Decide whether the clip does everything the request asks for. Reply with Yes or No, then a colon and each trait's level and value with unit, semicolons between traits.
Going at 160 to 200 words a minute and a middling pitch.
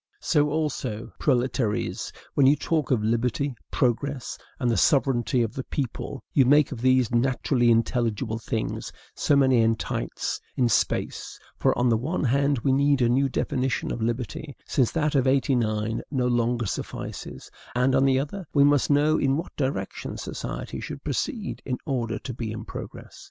No: average, 165 wpm; low, 130 Hz